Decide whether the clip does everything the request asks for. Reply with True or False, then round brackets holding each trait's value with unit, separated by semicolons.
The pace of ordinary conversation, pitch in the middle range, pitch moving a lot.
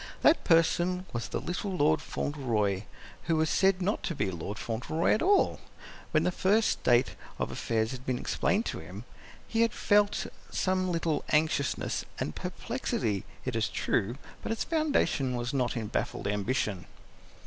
True (160 wpm; 150 Hz; 8.1 semitones)